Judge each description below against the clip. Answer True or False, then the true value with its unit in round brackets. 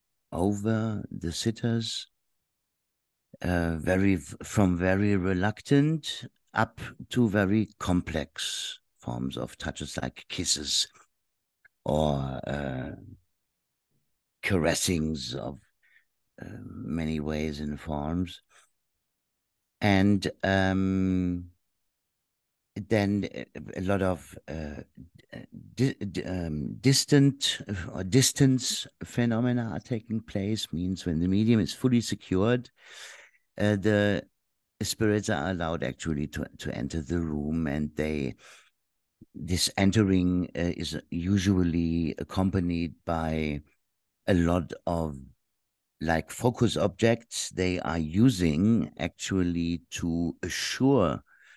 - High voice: False (90 Hz)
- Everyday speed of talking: False (95 wpm)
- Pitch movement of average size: True (4.7 semitones)